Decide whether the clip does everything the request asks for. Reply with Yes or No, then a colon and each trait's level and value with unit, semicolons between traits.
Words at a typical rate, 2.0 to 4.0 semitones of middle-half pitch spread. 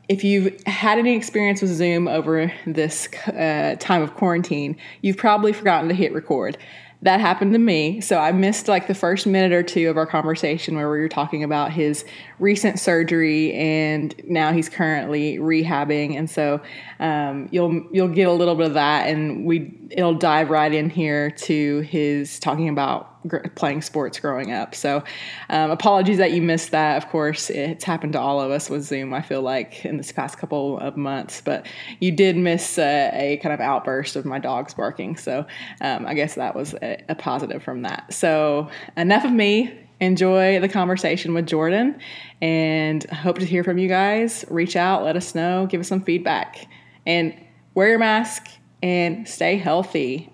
Yes: average, 185 wpm; average, 3.5 semitones